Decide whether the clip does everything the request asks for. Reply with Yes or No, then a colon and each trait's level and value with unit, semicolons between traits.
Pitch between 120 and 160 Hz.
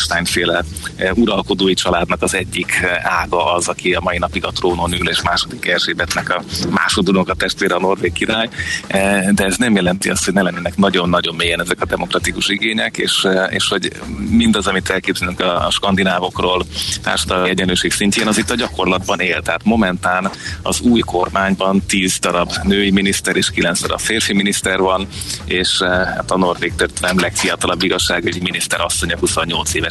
No: very low, 95 Hz